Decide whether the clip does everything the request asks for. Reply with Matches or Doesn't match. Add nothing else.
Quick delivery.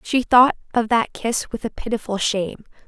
Doesn't match